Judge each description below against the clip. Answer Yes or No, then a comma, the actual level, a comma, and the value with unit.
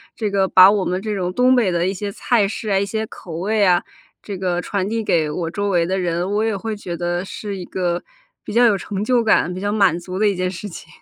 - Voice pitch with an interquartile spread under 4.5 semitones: Yes, average, 2.8 semitones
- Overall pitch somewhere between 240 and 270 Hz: No, high, 195 Hz